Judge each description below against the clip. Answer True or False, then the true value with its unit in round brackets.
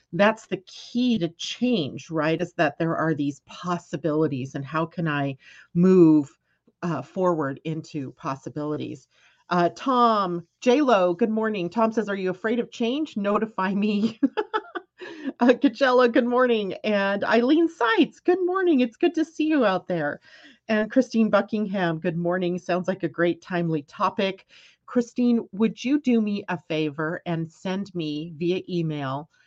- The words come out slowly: False (150 wpm)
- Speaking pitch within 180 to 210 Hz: True (190 Hz)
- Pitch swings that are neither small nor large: False (6.2 semitones)